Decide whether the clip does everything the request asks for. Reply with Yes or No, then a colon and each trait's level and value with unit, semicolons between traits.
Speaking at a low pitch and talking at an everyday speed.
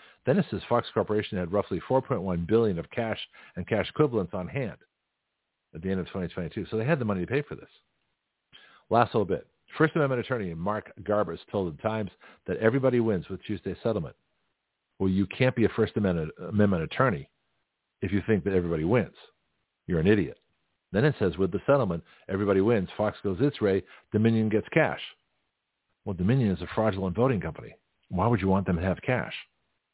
Yes: low, 100 Hz; average, 190 wpm